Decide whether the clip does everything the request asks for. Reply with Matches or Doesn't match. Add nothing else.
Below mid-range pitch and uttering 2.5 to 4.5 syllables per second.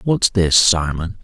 Matches